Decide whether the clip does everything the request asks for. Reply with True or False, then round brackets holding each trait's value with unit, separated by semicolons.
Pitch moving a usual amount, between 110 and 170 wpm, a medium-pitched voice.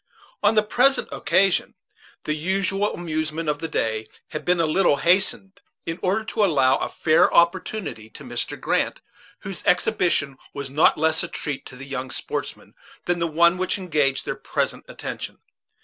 True (4.5 semitones; 165 wpm; 165 Hz)